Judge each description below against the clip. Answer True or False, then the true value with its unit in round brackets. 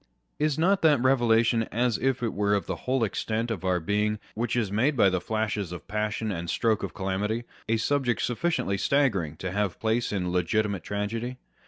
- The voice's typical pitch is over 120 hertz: False (110 Hz)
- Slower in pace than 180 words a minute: False (190 wpm)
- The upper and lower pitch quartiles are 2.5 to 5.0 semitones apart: True (3.3 semitones)